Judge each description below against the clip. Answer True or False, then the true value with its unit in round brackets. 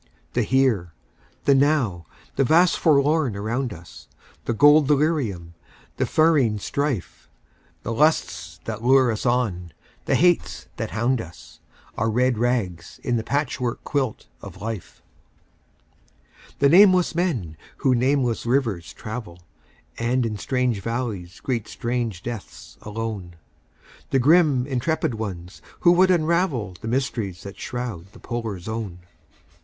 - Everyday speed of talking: False (130 wpm)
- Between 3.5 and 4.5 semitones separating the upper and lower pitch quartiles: False (5.2 semitones)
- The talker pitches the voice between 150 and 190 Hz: False (120 Hz)